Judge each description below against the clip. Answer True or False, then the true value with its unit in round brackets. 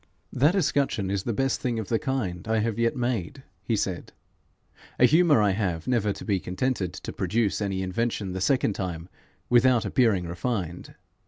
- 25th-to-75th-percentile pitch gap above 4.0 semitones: True (4.9 semitones)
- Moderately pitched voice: False (110 Hz)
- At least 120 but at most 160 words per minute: False (175 wpm)